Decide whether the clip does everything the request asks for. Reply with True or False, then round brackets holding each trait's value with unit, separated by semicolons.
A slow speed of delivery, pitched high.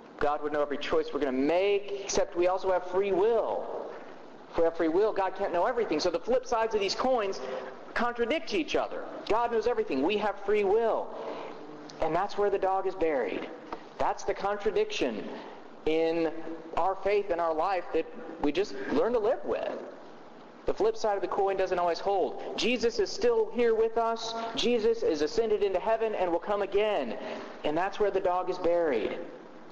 False (190 wpm; 205 Hz)